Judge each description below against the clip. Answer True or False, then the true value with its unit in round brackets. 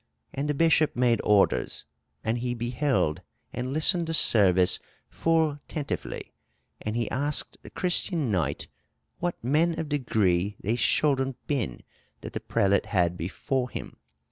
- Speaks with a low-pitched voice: True (125 Hz)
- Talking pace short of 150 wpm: True (140 wpm)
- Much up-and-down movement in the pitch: True (6.3 semitones)